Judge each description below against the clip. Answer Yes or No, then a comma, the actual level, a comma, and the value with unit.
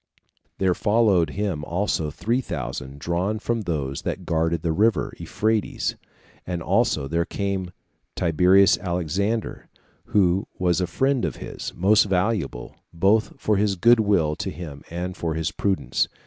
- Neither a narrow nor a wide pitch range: Yes, average, 4.1 semitones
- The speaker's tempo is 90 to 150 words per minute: Yes, average, 145 wpm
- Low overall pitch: Yes, very low, 90 Hz